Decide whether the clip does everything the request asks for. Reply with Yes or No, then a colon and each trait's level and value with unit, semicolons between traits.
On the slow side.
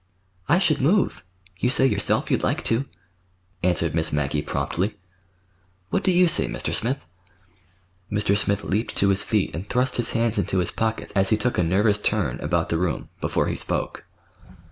No: average, 180 wpm